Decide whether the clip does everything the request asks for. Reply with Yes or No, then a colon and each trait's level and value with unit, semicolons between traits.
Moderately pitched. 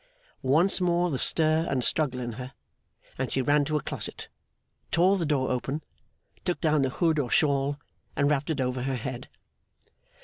Yes: medium, 145 Hz